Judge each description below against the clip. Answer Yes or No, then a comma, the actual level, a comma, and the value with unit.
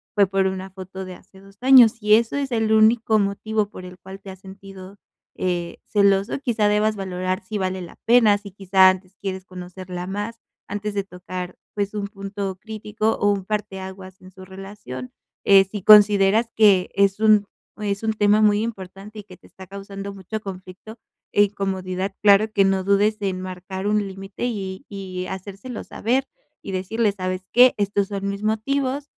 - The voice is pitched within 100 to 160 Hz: No, high, 200 Hz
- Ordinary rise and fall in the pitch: No, narrow, 2.0 semitones